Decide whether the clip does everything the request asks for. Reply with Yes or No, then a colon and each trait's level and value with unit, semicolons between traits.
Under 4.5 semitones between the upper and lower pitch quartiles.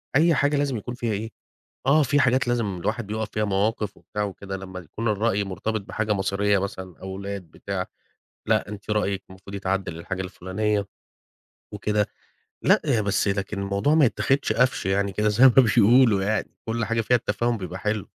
Yes: average, 2.7 semitones